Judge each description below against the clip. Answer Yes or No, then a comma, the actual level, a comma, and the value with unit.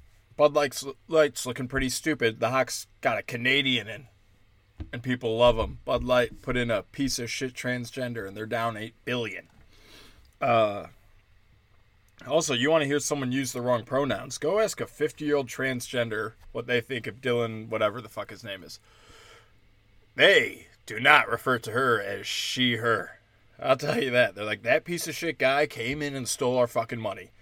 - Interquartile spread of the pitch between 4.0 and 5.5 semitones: No, average, 3.4 semitones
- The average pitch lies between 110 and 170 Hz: Yes, low, 125 Hz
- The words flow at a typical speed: Yes, average, 180 wpm